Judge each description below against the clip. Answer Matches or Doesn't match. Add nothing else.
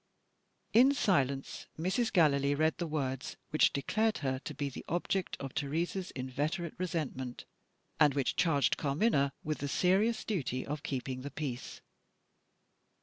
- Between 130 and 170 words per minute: Matches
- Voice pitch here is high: Doesn't match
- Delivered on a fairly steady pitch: Doesn't match